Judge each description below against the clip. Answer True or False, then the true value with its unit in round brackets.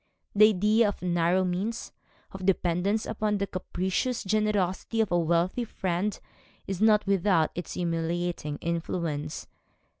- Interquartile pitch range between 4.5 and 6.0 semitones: False (3.5 semitones)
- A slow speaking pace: True (125 wpm)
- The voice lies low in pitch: False (185 Hz)